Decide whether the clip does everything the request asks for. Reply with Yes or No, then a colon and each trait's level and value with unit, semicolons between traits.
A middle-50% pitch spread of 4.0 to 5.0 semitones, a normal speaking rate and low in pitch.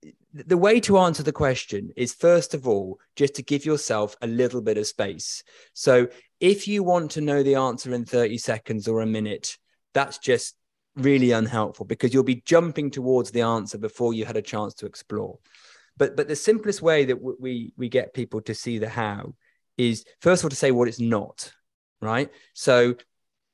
Yes: average, 4.6 semitones; average, 195 wpm; low, 125 Hz